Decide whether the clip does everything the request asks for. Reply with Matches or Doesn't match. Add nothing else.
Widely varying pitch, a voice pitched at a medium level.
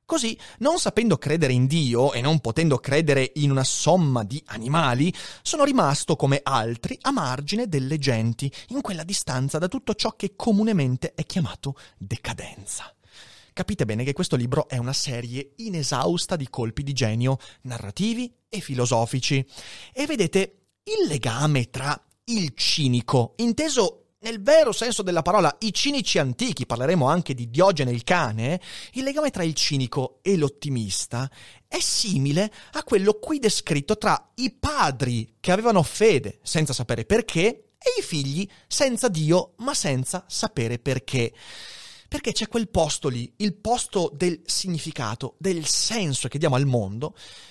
Matches